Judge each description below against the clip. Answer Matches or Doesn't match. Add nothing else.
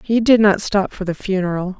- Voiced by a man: Doesn't match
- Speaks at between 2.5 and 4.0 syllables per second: Doesn't match